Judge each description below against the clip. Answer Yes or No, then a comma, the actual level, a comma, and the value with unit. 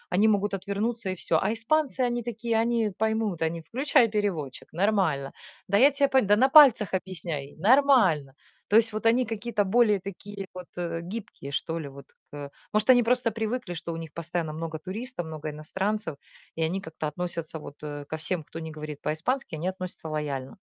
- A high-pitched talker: Yes, high, 195 Hz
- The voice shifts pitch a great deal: Yes, wide, 6.1 semitones